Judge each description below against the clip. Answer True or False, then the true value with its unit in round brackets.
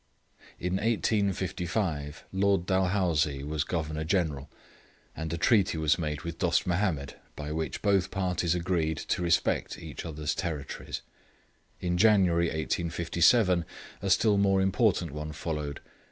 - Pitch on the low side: True (85 Hz)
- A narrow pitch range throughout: False (3.5 semitones)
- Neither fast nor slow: False (125 wpm)